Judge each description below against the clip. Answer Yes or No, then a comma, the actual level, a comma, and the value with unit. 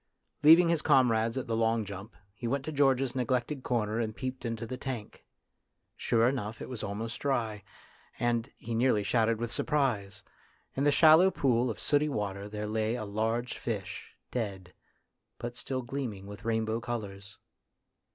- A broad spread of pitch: No, average, 3.3 semitones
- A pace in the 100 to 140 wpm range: No, average, 160 wpm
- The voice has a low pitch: Yes, low, 115 Hz